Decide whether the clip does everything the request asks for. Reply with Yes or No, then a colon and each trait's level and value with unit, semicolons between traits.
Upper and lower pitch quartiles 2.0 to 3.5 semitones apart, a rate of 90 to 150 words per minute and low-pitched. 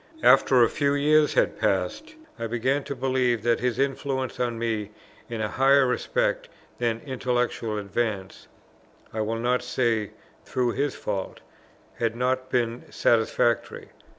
Yes: narrow, 2.4 semitones; average, 140 wpm; low, 120 Hz